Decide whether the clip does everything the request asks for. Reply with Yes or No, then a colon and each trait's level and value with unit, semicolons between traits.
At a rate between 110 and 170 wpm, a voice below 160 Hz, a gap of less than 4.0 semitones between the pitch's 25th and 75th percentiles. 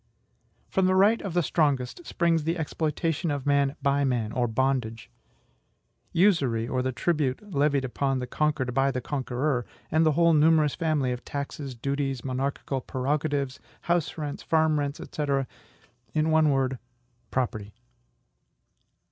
Yes: average, 140 wpm; medium, 140 Hz; average, 3.4 semitones